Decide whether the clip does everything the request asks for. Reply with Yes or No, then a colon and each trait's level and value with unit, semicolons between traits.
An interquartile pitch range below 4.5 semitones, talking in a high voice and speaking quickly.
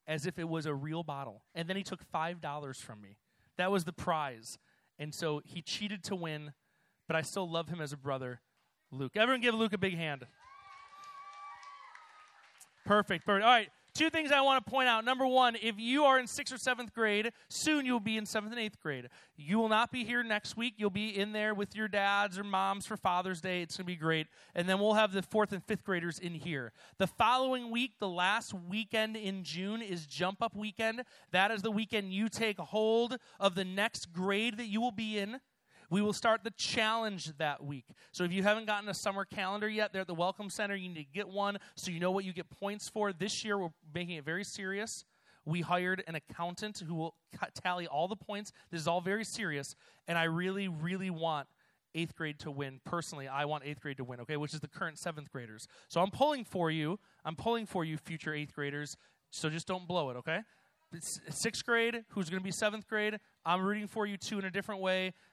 No: average, 4.8 semitones; high, 195 Hz; fast, 225 wpm